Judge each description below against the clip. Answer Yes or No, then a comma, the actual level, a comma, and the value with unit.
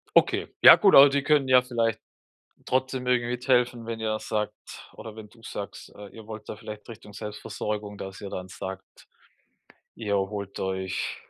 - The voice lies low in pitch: Yes, low, 110 Hz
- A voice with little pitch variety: No, average, 3.3 semitones